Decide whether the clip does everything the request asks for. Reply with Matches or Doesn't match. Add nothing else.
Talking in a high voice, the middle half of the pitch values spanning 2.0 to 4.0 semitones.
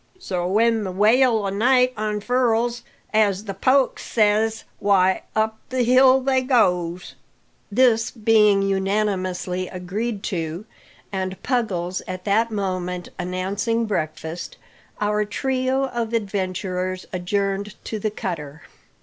Matches